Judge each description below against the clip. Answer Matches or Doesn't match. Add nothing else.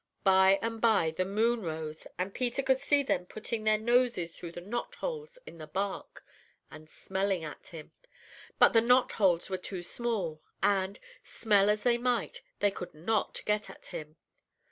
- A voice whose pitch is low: Doesn't match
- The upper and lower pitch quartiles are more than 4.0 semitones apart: Matches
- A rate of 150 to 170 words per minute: Matches